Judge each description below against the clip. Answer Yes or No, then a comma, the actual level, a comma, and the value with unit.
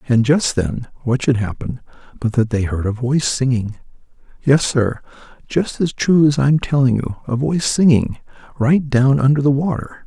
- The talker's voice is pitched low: Yes, low, 130 Hz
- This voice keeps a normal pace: Yes, average, 180 wpm